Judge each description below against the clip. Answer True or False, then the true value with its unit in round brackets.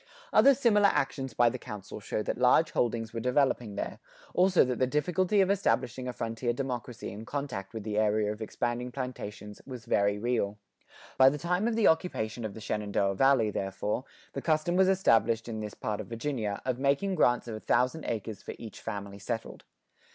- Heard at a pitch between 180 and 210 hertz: False (120 Hz)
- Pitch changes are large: False (4.7 semitones)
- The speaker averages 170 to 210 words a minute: True (190 wpm)